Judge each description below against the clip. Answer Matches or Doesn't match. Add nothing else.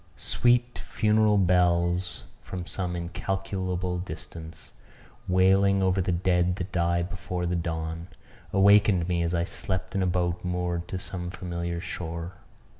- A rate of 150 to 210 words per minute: Doesn't match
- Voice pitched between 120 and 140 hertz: Doesn't match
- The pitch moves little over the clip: Matches